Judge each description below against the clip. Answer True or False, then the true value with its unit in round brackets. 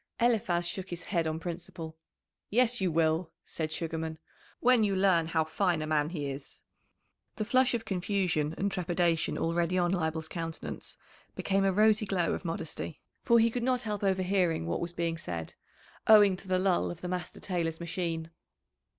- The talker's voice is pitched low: False (175 Hz)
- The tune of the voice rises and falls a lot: False (3.3 semitones)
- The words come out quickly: False (175 wpm)